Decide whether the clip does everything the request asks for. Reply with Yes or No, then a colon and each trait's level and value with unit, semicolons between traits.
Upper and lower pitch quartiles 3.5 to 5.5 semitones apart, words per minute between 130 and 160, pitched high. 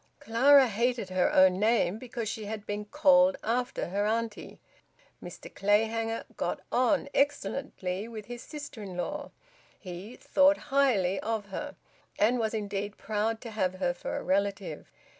Yes: average, 3.9 semitones; average, 150 wpm; high, 220 Hz